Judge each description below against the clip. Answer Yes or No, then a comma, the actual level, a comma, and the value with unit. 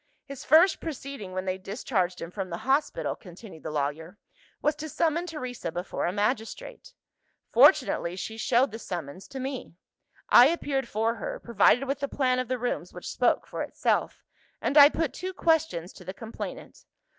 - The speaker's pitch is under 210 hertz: No, high, 245 Hz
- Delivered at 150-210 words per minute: Yes, average, 175 wpm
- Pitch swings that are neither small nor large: No, wide, 7.2 semitones